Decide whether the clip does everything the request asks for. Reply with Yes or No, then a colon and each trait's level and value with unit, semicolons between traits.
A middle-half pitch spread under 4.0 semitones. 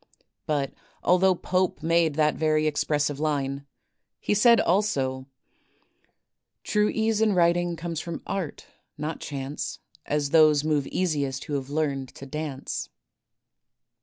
Yes: average, 3.6 semitones